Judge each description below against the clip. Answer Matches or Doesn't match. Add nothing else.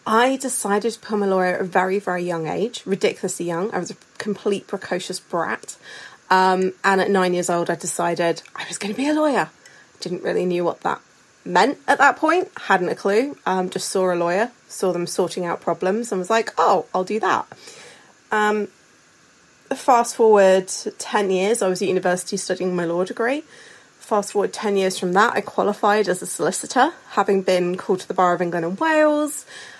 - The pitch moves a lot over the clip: Doesn't match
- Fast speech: Doesn't match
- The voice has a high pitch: Matches